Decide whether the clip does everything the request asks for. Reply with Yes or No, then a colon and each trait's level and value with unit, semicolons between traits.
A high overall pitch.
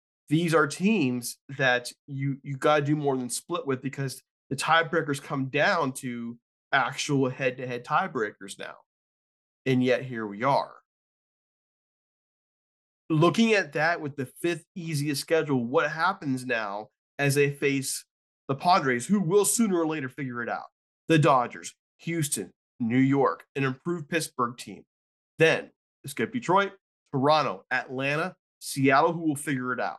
No: medium, 140 Hz